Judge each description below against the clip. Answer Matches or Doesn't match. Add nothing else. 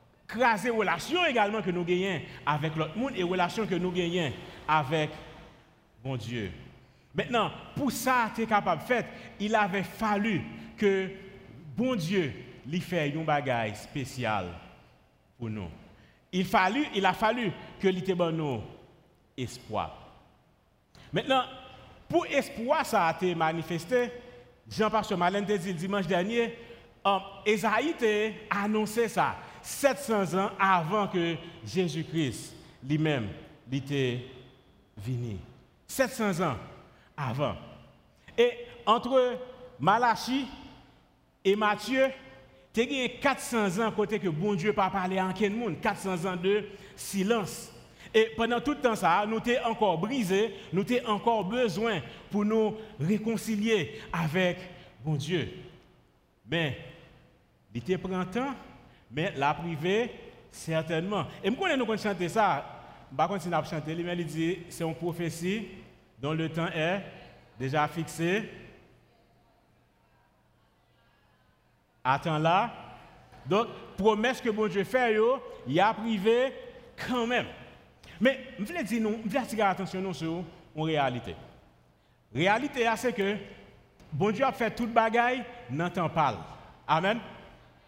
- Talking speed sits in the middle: Doesn't match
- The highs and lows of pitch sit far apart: Matches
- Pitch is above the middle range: Matches